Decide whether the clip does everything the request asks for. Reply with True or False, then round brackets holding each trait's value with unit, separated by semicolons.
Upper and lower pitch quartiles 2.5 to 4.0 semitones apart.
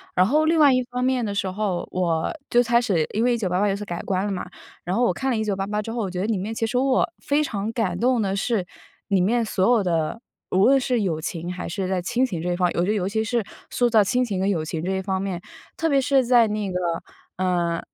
False (4.6 semitones)